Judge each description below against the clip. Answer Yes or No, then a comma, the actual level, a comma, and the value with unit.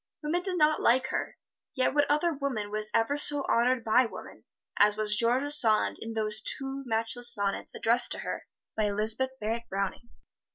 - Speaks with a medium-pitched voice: No, high, 235 Hz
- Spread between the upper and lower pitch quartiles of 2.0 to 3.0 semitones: No, average, 4.2 semitones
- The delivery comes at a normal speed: Yes, average, 175 wpm